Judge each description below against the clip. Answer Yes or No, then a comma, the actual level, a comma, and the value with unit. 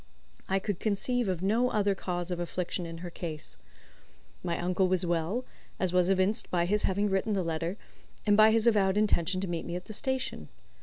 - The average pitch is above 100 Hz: Yes, high, 190 Hz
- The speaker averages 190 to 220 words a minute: Yes, average, 200 wpm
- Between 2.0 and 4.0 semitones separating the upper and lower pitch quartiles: Yes, average, 3.1 semitones